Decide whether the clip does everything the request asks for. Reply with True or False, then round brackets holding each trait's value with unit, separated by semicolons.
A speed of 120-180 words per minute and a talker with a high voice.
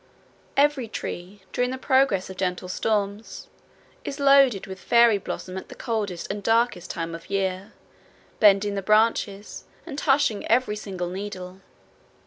True (140 wpm; 205 Hz)